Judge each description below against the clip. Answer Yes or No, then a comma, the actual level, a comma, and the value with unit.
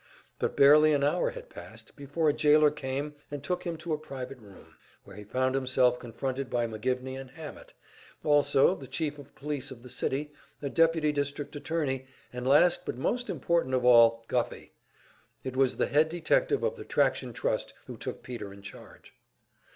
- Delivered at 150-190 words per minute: Yes, average, 180 wpm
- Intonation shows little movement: No, average, 3.3 semitones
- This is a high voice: No, medium, 140 Hz